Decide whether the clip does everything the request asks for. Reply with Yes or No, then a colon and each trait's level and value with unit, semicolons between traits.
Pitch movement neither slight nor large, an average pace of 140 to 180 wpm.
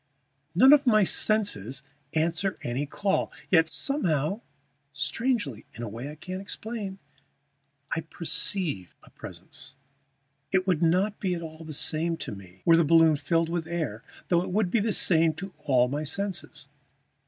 Yes: average, 4.6 semitones; average, 160 wpm